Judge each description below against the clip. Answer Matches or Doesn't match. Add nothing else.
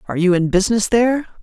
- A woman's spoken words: Matches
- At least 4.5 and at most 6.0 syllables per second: Doesn't match